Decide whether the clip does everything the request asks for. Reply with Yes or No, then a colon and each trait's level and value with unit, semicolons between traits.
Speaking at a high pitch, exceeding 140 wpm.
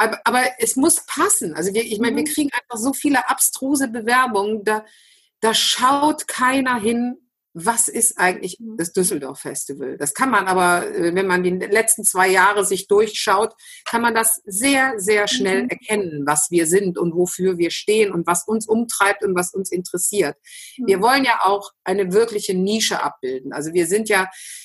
Yes: high, 215 Hz; average, 175 wpm